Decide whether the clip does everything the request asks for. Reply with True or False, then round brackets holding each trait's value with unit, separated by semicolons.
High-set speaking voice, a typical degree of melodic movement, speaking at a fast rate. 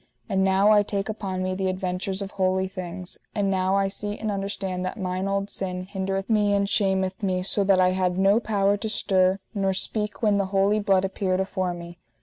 False (195 Hz; 1.3 semitones; 210 wpm)